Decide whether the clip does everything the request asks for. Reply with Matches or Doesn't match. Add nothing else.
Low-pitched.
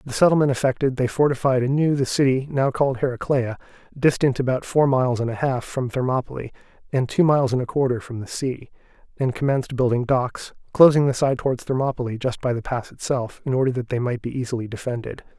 Matches